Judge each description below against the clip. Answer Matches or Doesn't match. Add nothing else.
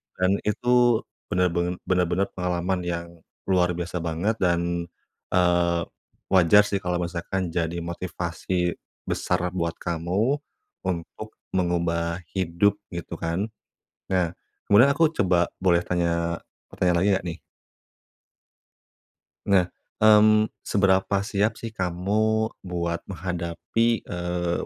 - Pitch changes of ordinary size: Doesn't match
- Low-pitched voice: Matches